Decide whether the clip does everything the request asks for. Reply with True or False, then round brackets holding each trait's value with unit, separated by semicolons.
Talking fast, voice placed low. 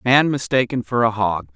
True (230 wpm; 115 Hz)